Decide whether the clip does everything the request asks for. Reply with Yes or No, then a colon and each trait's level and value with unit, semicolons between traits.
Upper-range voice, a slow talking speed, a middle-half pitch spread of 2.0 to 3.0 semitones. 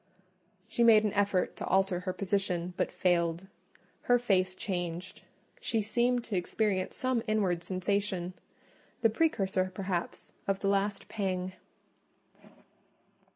Yes: high, 195 Hz; slow, 115 wpm; average, 2.7 semitones